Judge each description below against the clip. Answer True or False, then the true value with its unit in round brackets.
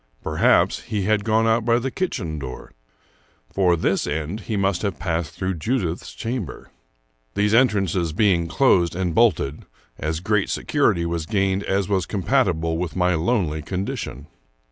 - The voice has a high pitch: False (95 Hz)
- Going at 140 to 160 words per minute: True (150 wpm)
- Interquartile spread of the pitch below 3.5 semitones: False (4.4 semitones)